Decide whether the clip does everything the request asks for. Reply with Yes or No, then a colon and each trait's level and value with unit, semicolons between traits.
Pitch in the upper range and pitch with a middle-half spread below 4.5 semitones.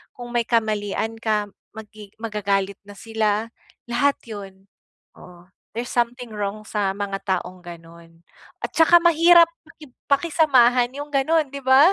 No: high, 220 Hz; average, 4.8 semitones